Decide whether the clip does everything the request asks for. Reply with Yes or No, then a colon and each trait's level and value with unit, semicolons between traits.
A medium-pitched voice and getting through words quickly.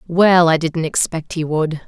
No: medium, 165 Hz; average, 190 wpm